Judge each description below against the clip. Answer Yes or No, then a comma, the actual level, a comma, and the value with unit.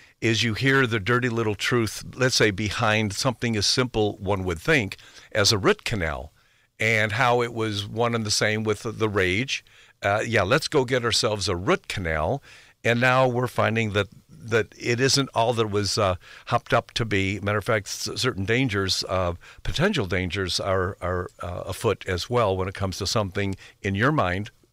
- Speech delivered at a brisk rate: No, average, 190 wpm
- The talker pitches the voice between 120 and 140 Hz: No, low, 110 Hz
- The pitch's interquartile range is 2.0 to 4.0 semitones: Yes, average, 3.3 semitones